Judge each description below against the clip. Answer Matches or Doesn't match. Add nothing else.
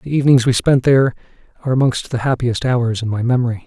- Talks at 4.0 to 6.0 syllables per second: Doesn't match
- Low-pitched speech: Matches